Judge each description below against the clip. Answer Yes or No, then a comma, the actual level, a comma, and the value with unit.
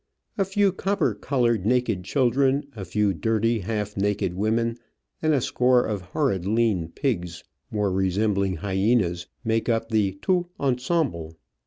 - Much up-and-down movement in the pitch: No, average, 4.6 semitones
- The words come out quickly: No, average, 140 wpm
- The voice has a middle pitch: No, low, 110 Hz